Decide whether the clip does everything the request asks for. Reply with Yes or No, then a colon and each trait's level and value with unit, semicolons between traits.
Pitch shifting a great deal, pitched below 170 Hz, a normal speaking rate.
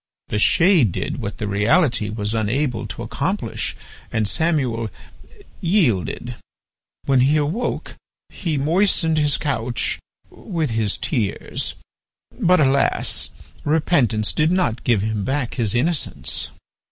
No: wide, 6.5 semitones; low, 135 Hz; slow, 115 wpm